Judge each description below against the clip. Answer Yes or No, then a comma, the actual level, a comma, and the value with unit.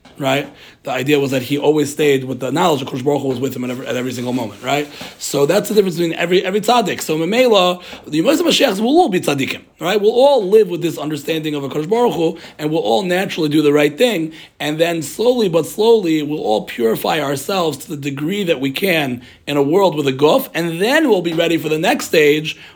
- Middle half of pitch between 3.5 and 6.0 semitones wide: Yes, average, 4.6 semitones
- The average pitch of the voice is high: No, medium, 160 Hz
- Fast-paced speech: Yes, fast, 250 wpm